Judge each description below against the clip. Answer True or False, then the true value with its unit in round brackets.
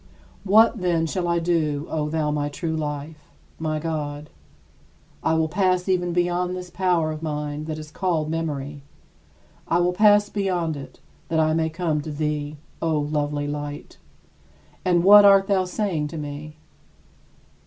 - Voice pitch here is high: False (160 Hz)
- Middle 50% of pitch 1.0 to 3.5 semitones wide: True (3.1 semitones)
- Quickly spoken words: False (155 wpm)